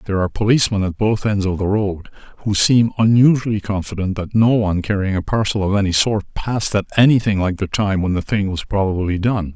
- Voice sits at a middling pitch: No, low, 100 Hz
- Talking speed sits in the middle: No, fast, 215 wpm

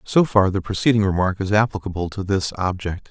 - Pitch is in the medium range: No, low, 100 Hz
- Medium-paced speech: Yes, average, 195 wpm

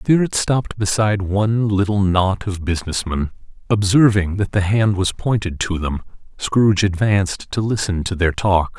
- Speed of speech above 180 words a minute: No, average, 170 wpm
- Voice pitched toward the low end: Yes, low, 100 Hz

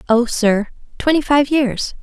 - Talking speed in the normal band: Yes, average, 150 wpm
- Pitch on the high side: Yes, very high, 250 Hz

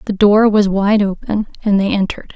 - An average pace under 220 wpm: Yes, fast, 205 wpm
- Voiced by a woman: Yes, female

